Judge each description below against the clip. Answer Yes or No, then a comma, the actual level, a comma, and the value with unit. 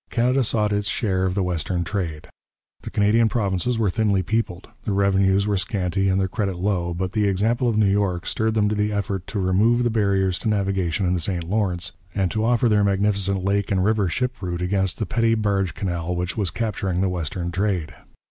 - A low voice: Yes, low, 100 Hz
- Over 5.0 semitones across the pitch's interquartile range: No, narrow, 2.5 semitones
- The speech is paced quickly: Yes, fast, 210 wpm